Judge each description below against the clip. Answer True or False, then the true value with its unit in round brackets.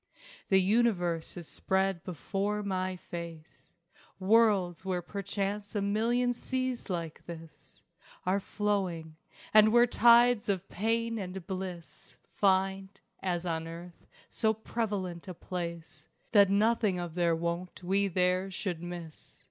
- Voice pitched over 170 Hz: True (190 Hz)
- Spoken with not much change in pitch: False (3.2 semitones)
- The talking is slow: True (125 wpm)